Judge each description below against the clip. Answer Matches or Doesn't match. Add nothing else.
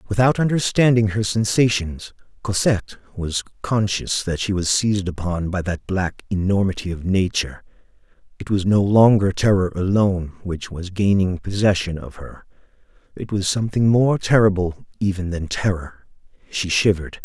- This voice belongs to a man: Matches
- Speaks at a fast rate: Doesn't match